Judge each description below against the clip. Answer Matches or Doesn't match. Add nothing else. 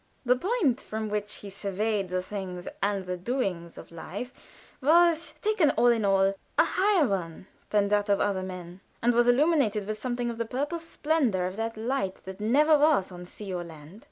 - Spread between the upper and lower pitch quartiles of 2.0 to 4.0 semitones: Doesn't match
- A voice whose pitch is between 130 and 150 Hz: Doesn't match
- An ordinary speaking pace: Matches